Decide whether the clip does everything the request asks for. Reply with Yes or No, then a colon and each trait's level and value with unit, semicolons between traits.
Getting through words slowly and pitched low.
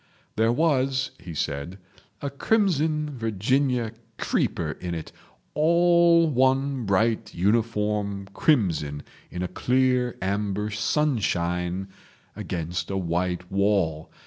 Yes: slow, 95 wpm; low, 105 Hz